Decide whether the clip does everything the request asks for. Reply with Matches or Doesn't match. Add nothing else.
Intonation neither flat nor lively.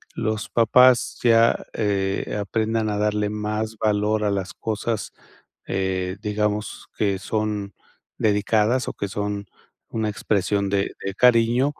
Doesn't match